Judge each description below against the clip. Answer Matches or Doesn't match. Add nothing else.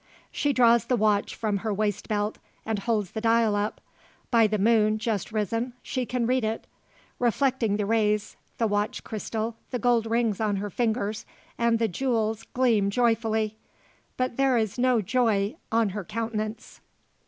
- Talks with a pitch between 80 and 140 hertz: Doesn't match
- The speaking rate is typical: Matches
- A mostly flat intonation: Matches